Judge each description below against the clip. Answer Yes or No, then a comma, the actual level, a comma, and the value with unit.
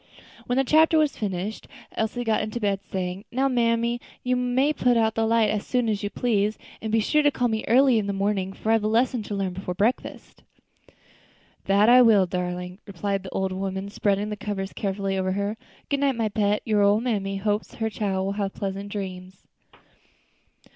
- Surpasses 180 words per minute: Yes, average, 200 wpm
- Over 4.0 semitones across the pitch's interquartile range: No, average, 3.1 semitones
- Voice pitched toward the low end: No, high, 210 Hz